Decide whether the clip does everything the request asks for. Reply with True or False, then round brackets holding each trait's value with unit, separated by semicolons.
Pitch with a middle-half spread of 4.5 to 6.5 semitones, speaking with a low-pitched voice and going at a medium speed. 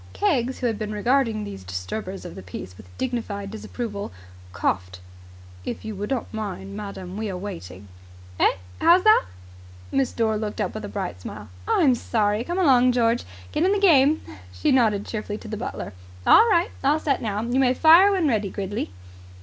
False (4.8 semitones; 220 Hz; 185 wpm)